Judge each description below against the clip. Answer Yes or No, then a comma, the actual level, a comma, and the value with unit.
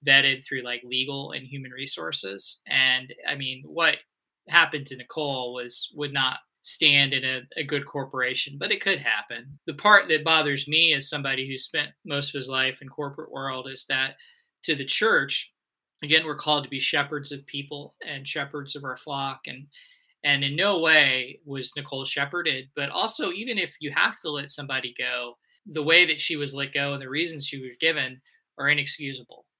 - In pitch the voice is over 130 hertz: Yes, medium, 140 Hz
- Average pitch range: No, narrow, 2.1 semitones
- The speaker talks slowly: No, average, 190 wpm